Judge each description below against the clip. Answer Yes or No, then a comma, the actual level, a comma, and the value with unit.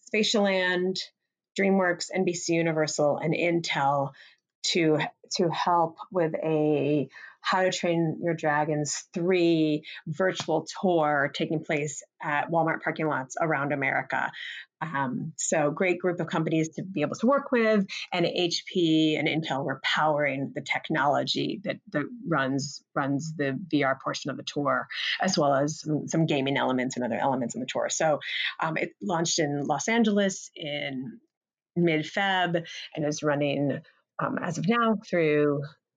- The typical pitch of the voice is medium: Yes, medium, 160 Hz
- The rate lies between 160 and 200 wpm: No, average, 145 wpm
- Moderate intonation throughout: Yes, average, 3.4 semitones